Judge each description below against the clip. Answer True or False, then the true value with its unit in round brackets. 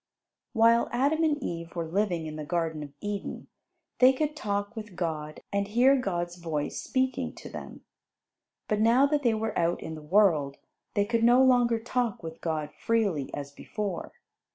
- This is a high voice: True (205 Hz)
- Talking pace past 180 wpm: False (175 wpm)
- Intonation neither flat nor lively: False (6.4 semitones)